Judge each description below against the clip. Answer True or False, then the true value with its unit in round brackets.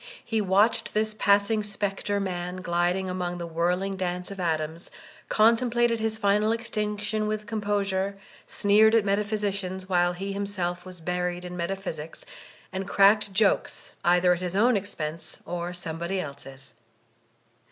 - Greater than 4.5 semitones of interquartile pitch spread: False (2.9 semitones)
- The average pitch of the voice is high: True (195 Hz)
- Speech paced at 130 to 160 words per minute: True (140 wpm)